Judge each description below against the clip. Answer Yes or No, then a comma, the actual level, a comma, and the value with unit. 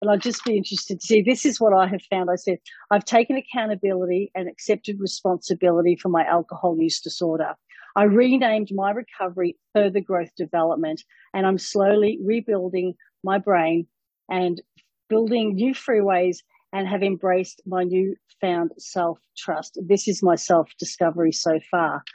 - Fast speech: No, average, 155 wpm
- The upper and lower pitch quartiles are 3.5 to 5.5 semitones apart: No, average, 2.9 semitones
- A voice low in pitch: No, high, 190 Hz